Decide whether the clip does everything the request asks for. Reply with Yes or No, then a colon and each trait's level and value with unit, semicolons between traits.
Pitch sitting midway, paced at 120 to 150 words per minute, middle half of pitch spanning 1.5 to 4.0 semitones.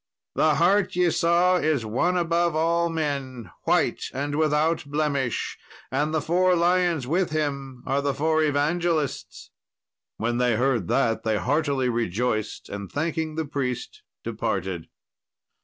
No: medium, 150 Hz; slow, 135 wpm; average, 4.4 semitones